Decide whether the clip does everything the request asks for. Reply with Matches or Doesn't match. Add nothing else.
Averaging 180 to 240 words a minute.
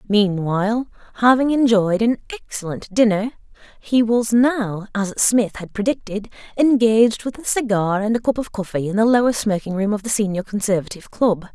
Doesn't match